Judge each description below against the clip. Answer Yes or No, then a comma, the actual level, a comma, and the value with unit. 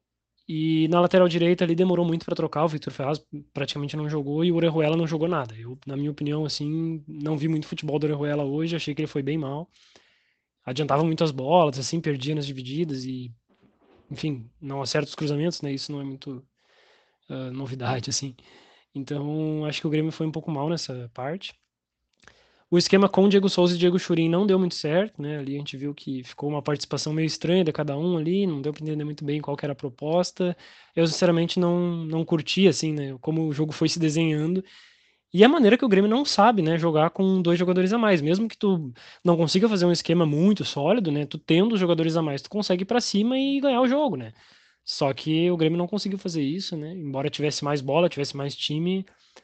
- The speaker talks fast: Yes, fast, 220 wpm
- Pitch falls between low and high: Yes, medium, 160 Hz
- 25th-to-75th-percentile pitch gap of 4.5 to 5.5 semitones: No, average, 3.4 semitones